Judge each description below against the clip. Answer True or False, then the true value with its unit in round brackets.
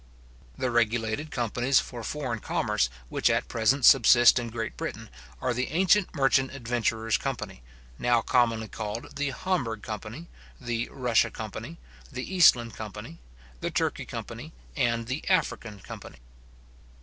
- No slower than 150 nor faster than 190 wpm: False (135 wpm)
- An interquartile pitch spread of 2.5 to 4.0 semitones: True (3.1 semitones)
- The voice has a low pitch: True (120 Hz)